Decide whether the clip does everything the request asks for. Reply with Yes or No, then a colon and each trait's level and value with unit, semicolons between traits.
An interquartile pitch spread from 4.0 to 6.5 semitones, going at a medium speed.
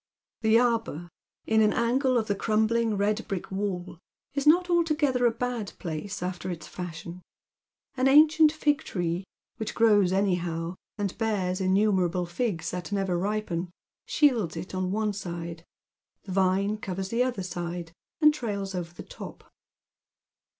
Yes: average, 4.5 semitones; average, 145 wpm